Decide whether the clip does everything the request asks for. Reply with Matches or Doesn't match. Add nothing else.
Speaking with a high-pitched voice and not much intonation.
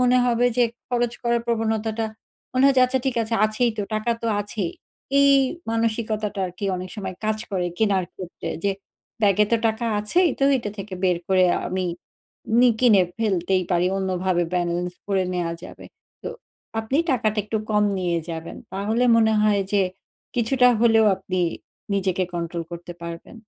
Doesn't match